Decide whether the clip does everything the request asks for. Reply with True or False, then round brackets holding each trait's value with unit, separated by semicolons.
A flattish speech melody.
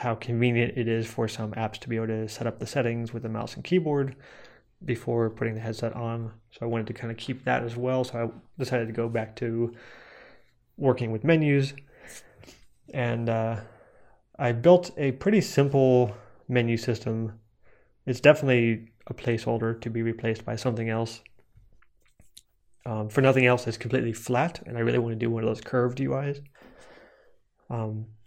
True (2.0 semitones)